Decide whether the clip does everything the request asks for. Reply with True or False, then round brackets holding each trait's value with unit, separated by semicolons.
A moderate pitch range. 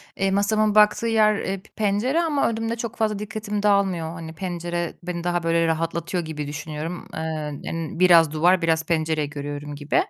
True (4.6 semitones)